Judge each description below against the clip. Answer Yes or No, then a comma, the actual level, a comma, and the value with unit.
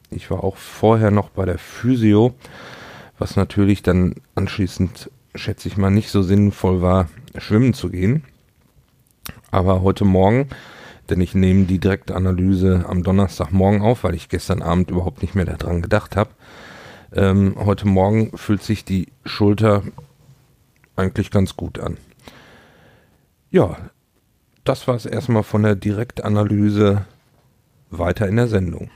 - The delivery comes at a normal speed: Yes, average, 135 wpm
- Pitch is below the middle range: Yes, low, 100 Hz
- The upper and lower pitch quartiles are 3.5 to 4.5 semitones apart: No, narrow, 2.6 semitones